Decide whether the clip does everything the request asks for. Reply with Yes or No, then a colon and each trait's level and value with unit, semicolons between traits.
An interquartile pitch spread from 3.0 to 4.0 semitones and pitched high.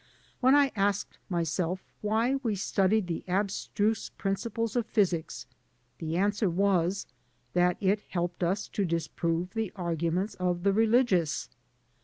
Yes: average, 3.4 semitones; high, 195 Hz